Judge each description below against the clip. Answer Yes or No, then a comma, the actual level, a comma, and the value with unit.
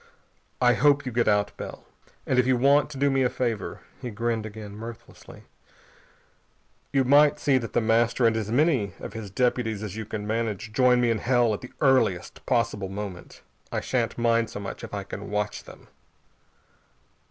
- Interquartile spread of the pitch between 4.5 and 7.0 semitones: No, average, 3.3 semitones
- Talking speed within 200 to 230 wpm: No, average, 185 wpm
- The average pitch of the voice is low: Yes, low, 115 Hz